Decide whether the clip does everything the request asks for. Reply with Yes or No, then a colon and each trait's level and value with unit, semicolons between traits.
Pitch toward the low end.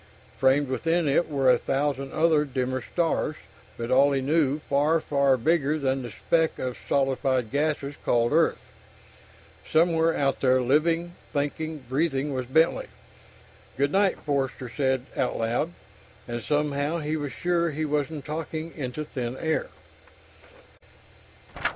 No: medium, 145 Hz